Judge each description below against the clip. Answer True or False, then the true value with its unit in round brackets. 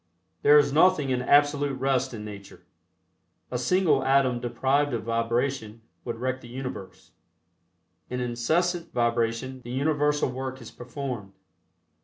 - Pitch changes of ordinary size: True (3.2 semitones)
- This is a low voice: True (130 Hz)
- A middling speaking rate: False (130 wpm)